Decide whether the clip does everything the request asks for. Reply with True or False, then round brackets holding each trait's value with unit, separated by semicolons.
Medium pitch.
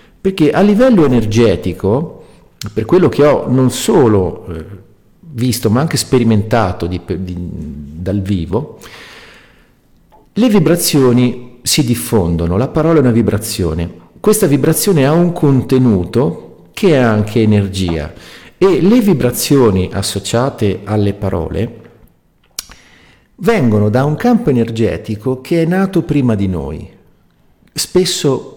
False (115 Hz)